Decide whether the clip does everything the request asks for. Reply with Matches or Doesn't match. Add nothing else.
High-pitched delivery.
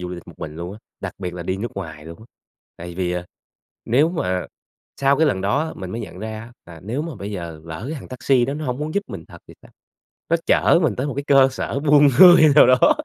Doesn't match